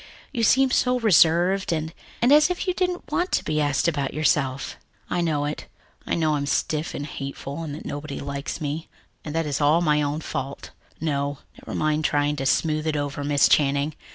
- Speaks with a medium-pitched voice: Yes, medium, 150 Hz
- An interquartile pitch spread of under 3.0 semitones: Yes, narrow, 2.6 semitones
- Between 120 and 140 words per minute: No, fast, 205 wpm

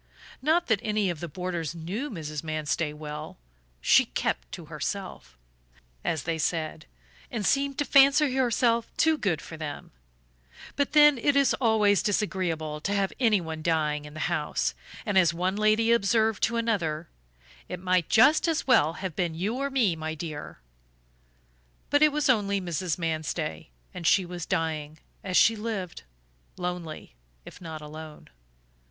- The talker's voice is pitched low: No, medium, 180 Hz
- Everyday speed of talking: Yes, average, 160 wpm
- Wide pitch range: Yes, wide, 6.3 semitones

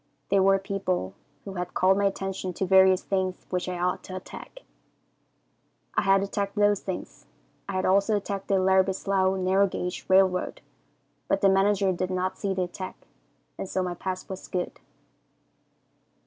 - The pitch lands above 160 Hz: Yes, high, 190 Hz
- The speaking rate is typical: Yes, average, 165 wpm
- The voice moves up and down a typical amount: No, narrow, 1.0 semitones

